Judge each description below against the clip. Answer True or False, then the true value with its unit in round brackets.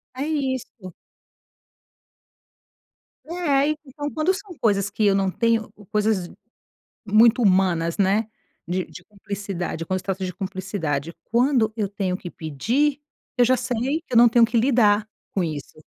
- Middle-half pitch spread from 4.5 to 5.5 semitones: True (5.1 semitones)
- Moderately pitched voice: False (210 Hz)